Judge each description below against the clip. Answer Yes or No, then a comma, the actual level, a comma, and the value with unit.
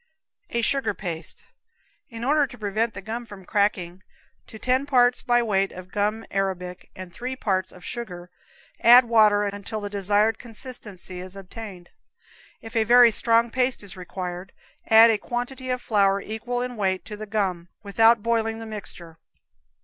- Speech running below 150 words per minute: No, average, 165 wpm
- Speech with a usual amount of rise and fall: Yes, average, 3.6 semitones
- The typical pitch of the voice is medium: No, high, 215 Hz